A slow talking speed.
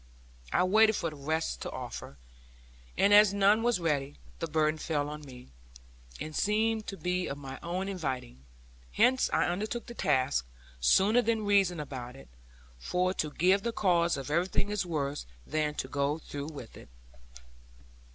No: average, 165 wpm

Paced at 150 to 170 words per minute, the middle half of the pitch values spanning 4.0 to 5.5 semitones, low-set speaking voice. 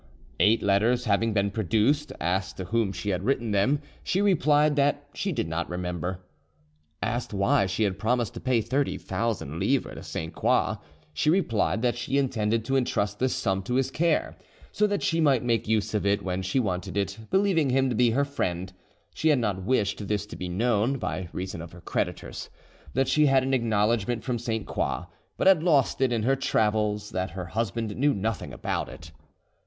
No: average, 195 wpm; average, 5.2 semitones; low, 110 Hz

